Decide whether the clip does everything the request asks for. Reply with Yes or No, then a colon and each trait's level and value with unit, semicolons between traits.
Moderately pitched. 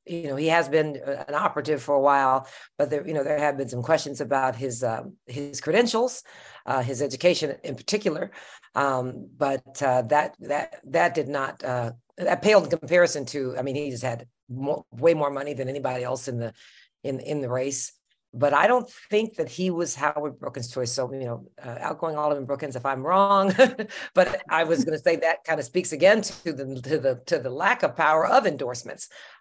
Yes: medium, 145 Hz